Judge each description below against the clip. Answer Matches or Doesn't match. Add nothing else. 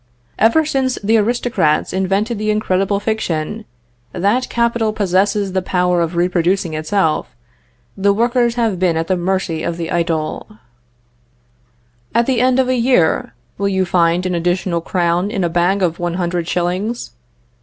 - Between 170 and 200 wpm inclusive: Doesn't match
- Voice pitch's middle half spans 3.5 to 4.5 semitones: Matches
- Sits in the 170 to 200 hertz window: Matches